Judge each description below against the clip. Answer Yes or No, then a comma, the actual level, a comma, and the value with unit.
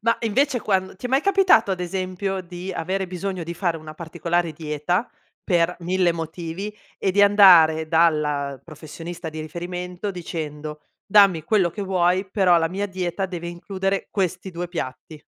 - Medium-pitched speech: Yes, medium, 180 Hz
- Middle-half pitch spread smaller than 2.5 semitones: No, average, 2.8 semitones